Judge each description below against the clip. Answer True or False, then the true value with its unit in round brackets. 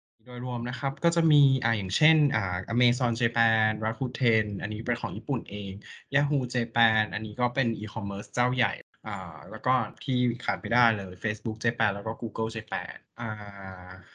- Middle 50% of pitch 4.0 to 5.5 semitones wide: False (2.4 semitones)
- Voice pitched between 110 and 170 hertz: True (115 Hz)